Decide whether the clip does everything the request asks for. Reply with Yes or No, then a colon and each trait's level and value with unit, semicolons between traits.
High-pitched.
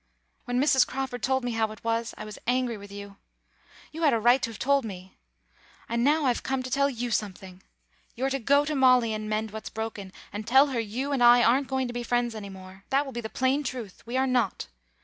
Yes: high, 240 Hz